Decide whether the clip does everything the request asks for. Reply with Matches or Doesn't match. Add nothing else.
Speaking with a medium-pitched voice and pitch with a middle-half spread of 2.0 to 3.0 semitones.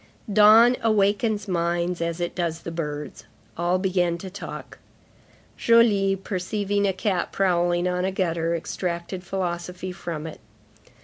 Matches